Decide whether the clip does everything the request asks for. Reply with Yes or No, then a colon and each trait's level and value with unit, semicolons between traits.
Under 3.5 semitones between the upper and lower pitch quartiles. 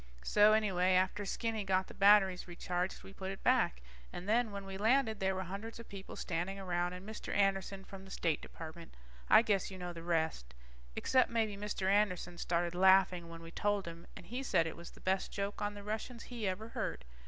Yes: average, 2.8 semitones